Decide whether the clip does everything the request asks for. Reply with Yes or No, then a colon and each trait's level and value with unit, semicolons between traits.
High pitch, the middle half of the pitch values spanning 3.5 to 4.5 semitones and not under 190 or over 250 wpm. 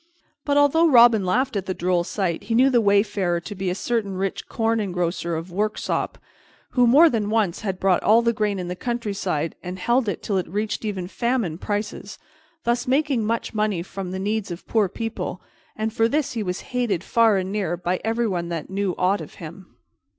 Yes: high, 205 Hz; average, 4.0 semitones; average, 200 wpm